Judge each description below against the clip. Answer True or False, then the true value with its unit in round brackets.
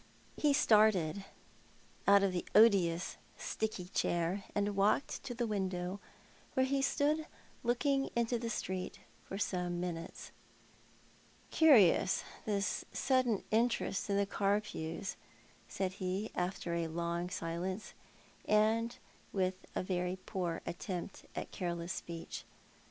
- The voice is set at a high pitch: True (195 Hz)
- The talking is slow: True (120 wpm)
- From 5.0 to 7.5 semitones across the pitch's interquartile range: False (3.7 semitones)